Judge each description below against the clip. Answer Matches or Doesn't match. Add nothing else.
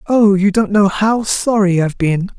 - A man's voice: Matches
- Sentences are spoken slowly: Doesn't match